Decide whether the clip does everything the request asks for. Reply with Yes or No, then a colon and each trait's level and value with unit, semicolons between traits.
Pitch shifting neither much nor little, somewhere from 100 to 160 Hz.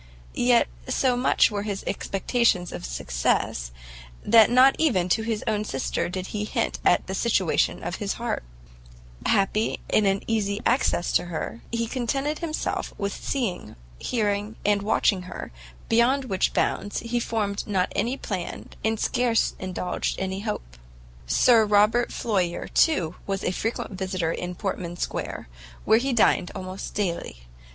No: average, 4.1 semitones; high, 205 Hz